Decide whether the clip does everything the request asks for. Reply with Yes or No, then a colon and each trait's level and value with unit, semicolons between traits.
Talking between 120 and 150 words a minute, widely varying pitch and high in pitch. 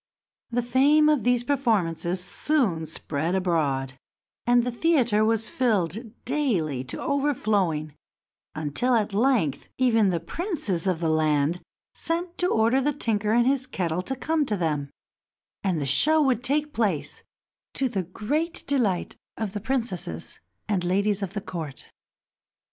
Yes: average, 145 wpm; wide, 7.4 semitones; high, 215 Hz